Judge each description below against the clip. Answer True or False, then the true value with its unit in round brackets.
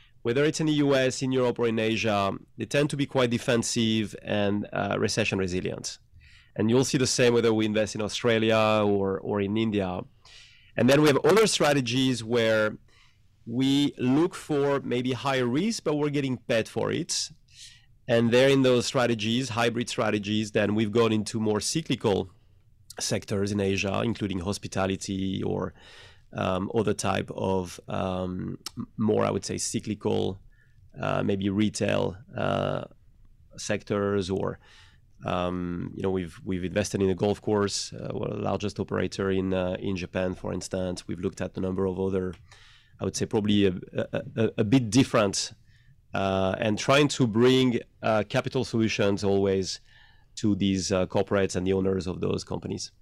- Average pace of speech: True (165 wpm)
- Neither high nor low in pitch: False (110 Hz)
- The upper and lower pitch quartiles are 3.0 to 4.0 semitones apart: True (3.7 semitones)